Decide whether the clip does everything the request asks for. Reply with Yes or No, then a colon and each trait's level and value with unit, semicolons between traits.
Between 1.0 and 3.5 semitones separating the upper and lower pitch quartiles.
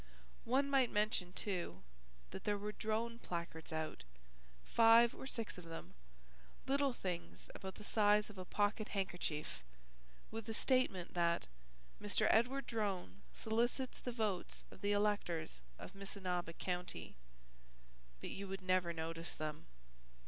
No: average, 4.2 semitones